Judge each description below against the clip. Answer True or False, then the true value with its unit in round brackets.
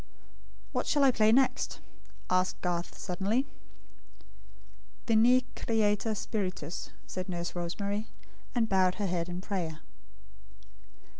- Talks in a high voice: True (200 Hz)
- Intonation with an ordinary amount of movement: True (3.8 semitones)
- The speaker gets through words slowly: True (105 wpm)